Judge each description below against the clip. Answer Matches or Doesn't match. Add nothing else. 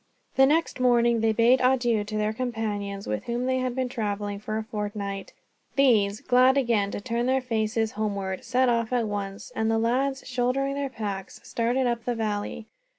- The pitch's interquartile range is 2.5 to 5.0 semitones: Matches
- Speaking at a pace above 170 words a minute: Matches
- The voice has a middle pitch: Doesn't match